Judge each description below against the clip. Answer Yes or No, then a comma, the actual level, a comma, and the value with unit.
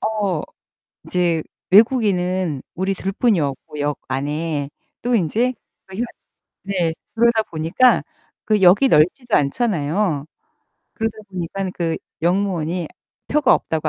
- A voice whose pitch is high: No, medium, 180 Hz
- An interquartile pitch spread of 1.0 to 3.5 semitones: No, average, 5.1 semitones